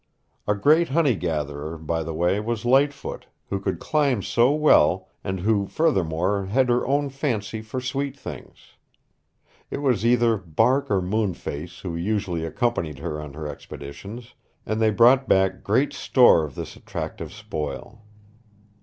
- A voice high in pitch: No, low, 105 Hz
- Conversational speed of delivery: Yes, average, 150 wpm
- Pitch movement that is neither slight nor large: No, wide, 6.9 semitones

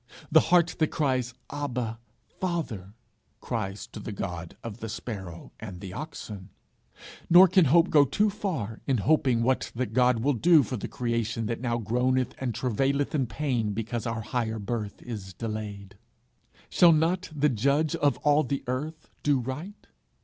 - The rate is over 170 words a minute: No, average, 165 wpm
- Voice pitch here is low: Yes, low, 125 Hz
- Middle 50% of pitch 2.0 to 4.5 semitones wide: No, average, 5.0 semitones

